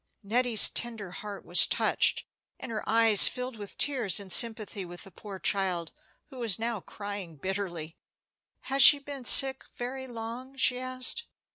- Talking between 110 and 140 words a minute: No, average, 155 wpm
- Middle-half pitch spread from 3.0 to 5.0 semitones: Yes, average, 4.6 semitones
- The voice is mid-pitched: No, high, 225 Hz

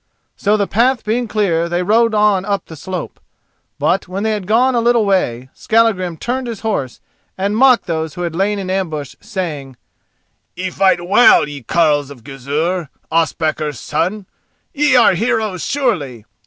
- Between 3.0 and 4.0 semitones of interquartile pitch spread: No, wide, 5.6 semitones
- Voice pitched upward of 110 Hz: Yes, high, 190 Hz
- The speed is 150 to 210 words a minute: Yes, average, 165 wpm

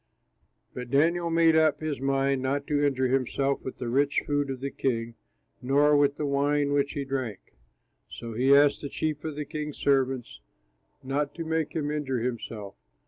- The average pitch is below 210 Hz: Yes, medium, 140 Hz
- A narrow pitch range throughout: Yes, narrow, 2.0 semitones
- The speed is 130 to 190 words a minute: Yes, average, 180 wpm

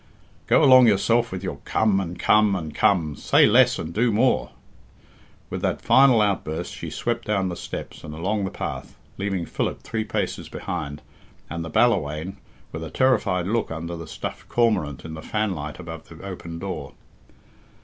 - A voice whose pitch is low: Yes, very low, 95 Hz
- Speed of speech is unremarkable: Yes, average, 170 wpm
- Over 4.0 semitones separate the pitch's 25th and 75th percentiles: Yes, average, 4.8 semitones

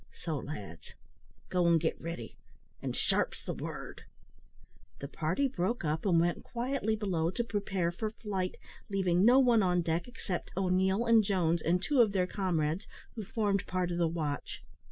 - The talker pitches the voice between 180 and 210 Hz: Yes, medium, 185 Hz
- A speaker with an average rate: Yes, average, 170 wpm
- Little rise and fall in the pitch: No, average, 4.0 semitones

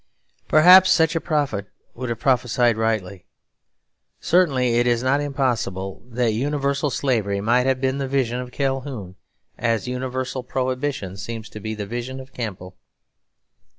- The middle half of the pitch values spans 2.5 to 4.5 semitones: Yes, average, 3.4 semitones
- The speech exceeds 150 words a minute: No, average, 145 wpm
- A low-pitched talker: Yes, low, 125 Hz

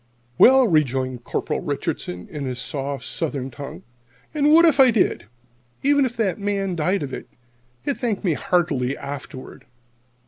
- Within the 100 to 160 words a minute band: Yes, average, 150 wpm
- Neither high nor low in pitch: Yes, medium, 165 Hz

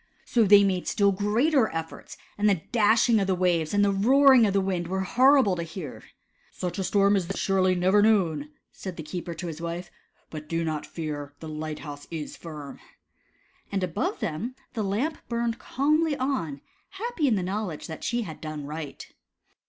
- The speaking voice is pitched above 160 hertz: Yes, high, 190 Hz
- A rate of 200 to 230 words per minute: Yes, fast, 205 wpm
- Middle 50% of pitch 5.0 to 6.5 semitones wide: Yes, average, 5.3 semitones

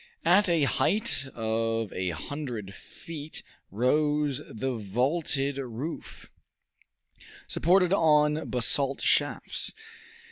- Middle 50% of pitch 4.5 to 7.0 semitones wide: Yes, wide, 5.4 semitones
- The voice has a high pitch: No, medium, 140 Hz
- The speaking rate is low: Yes, slow, 85 wpm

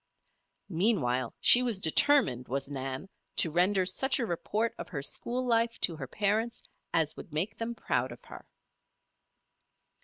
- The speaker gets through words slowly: No, average, 150 wpm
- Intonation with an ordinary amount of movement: No, wide, 7.6 semitones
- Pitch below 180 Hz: No, high, 190 Hz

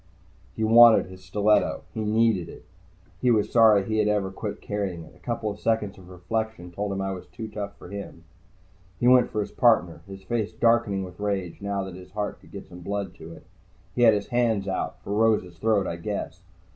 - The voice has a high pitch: No, low, 100 Hz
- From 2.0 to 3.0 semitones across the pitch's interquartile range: Yes, average, 2.7 semitones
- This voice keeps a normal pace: No, fast, 210 wpm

